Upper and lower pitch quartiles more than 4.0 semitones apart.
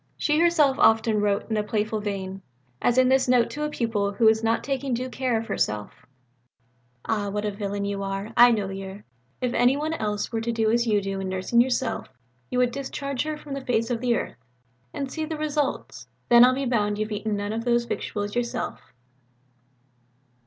No: average, 3.7 semitones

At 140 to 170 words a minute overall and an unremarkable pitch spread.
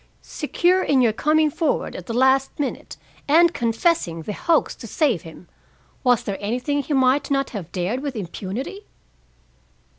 No: average, 155 wpm; wide, 6.1 semitones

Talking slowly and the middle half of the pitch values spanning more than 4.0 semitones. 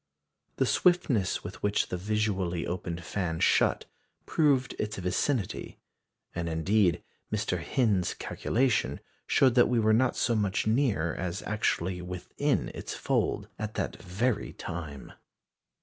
Yes: slow, 130 wpm; average, 4.5 semitones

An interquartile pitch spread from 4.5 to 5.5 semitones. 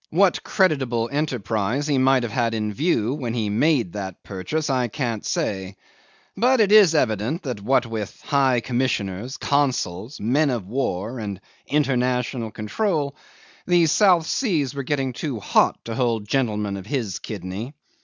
Yes: average, 5.2 semitones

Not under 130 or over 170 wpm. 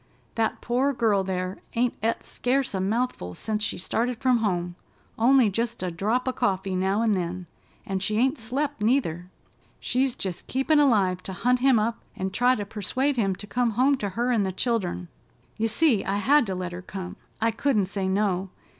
No: average, 190 wpm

